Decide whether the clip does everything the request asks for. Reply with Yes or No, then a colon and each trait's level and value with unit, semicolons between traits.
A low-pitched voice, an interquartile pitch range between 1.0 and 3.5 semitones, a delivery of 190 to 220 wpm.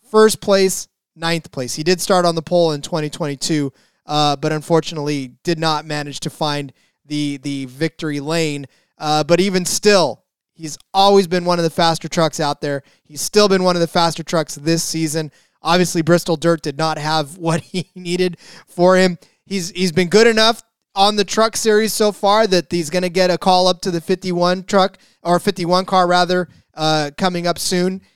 No: medium, 170 Hz; average, 3.1 semitones; average, 200 wpm